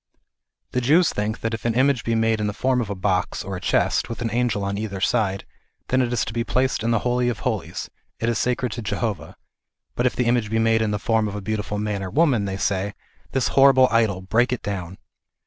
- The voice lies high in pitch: No, low, 115 Hz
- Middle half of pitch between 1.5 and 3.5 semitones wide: Yes, average, 3.0 semitones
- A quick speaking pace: Yes, fast, 250 wpm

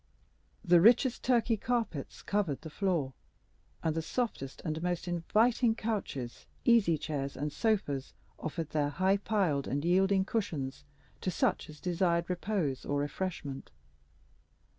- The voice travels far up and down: Yes, wide, 6.0 semitones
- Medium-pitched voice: Yes, medium, 175 Hz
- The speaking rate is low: Yes, slow, 130 wpm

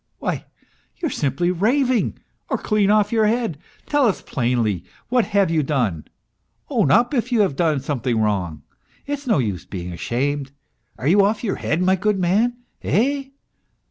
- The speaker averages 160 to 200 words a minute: Yes, average, 175 wpm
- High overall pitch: No, medium, 180 Hz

